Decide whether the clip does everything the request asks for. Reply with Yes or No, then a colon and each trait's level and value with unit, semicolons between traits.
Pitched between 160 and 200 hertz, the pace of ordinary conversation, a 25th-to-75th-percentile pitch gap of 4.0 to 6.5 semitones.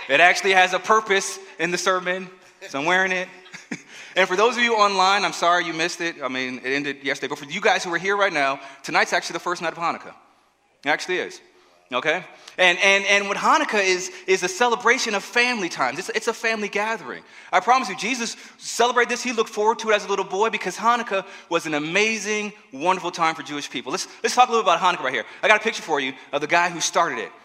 No: high, 190 Hz; fast, 245 wpm; average, 4.3 semitones